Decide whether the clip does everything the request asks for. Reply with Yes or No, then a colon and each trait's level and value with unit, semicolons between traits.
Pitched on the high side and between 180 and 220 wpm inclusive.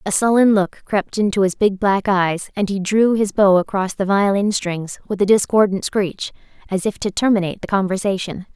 Yes: high, 195 Hz; average, 195 wpm